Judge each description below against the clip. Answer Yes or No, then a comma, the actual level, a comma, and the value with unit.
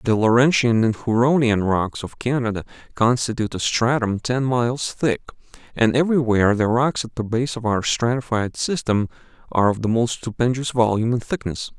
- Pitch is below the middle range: Yes, low, 120 Hz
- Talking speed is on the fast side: No, average, 165 wpm